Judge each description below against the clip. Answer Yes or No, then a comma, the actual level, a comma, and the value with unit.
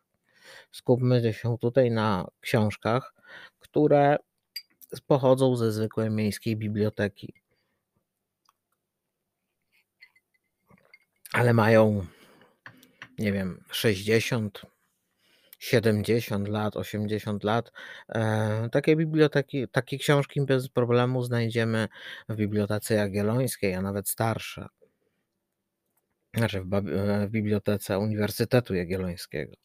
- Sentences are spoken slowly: Yes, slow, 75 wpm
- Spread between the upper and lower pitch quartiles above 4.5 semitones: No, average, 2.9 semitones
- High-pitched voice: No, low, 110 Hz